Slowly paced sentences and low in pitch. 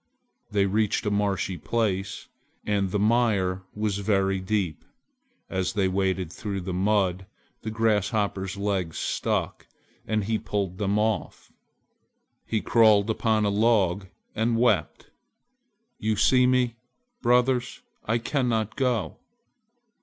Yes: slow, 120 wpm; low, 105 Hz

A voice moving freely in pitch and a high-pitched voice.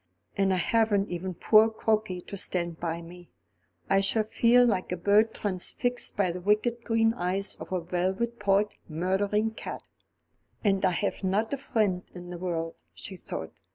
No: average, 3.5 semitones; high, 195 Hz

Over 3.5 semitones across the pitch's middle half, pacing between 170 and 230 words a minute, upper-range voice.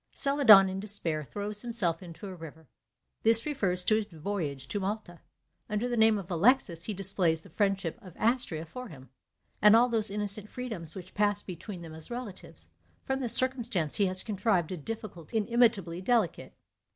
Yes: average, 4.5 semitones; average, 175 wpm; high, 200 Hz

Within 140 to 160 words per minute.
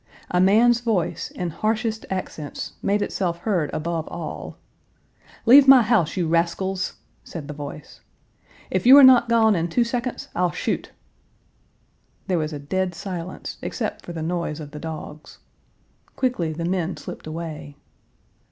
Yes: average, 150 wpm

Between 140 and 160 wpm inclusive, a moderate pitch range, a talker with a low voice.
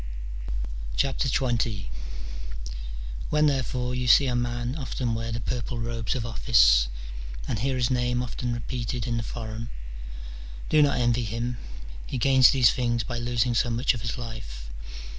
No: average, 150 wpm; narrow, 1.5 semitones; low, 120 Hz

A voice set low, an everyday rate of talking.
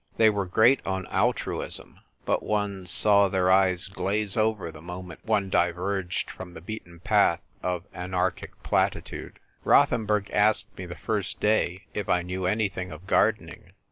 Yes: very low, 95 Hz; average, 150 wpm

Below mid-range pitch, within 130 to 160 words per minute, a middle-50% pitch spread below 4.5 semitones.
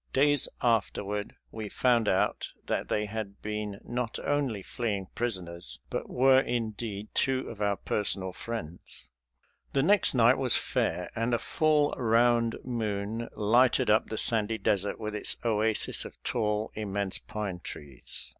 Yes: low, 110 Hz; average, 145 wpm; average, 2.9 semitones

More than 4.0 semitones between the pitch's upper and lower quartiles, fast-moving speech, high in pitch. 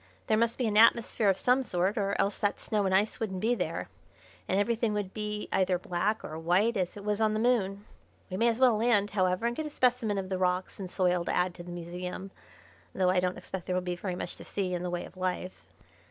No: average, 3.2 semitones; fast, 250 wpm; high, 195 Hz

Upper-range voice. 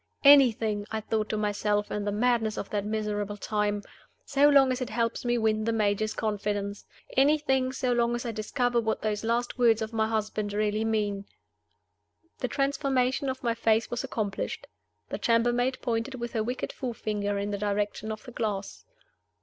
Yes: high, 220 Hz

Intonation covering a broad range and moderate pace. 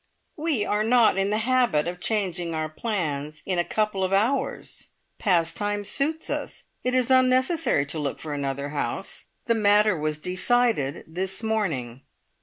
Yes: wide, 6.8 semitones; average, 155 wpm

